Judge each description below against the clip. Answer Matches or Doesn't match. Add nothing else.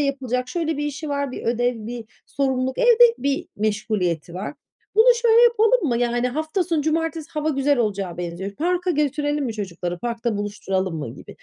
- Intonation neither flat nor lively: Doesn't match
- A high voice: Matches